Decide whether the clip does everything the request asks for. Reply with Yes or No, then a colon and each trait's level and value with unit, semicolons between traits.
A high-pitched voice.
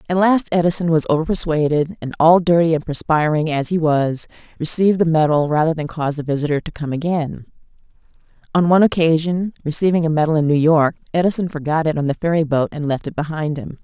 No: medium, 160 Hz